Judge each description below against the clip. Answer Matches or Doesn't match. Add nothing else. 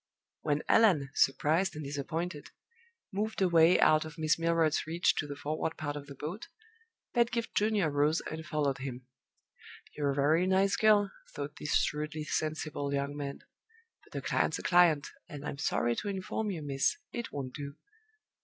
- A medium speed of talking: Matches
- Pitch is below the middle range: Doesn't match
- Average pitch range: Matches